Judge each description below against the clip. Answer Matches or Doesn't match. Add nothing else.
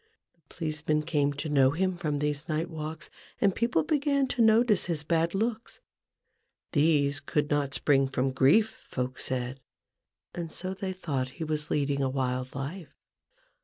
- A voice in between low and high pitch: Matches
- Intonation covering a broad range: Doesn't match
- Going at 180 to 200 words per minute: Doesn't match